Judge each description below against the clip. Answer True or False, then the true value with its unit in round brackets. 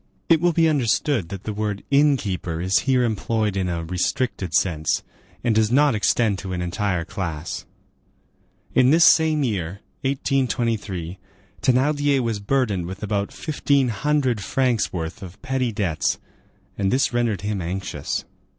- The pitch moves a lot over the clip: True (5.9 semitones)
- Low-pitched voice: True (110 Hz)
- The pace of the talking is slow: False (150 wpm)